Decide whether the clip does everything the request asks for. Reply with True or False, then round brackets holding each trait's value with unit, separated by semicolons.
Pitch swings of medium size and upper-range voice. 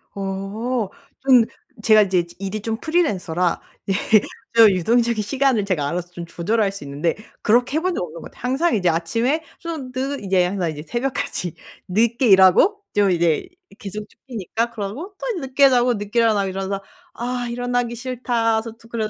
True (4.6 semitones; 220 Hz)